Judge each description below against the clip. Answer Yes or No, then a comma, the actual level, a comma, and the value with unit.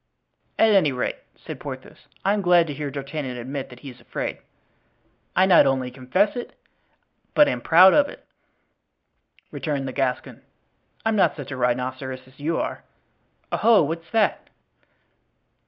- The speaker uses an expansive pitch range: Yes, wide, 6.2 semitones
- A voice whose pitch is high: No, medium, 145 Hz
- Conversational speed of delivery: Yes, average, 155 wpm